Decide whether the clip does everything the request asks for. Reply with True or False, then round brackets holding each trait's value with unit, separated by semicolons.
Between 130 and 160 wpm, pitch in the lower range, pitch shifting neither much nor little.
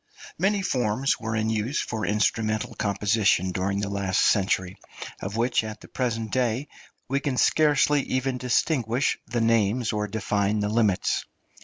True (150 wpm; 110 Hz; 3.5 semitones)